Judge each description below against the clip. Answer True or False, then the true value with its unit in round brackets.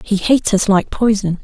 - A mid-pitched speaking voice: False (205 Hz)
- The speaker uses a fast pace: True (210 wpm)